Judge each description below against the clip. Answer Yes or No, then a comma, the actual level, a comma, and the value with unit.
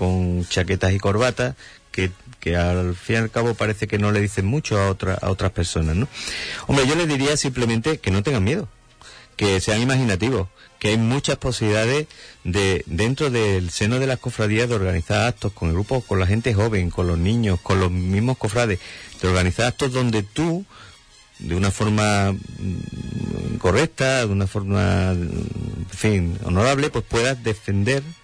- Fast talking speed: No, average, 170 wpm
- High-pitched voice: No, low, 105 Hz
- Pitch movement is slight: No, average, 4.5 semitones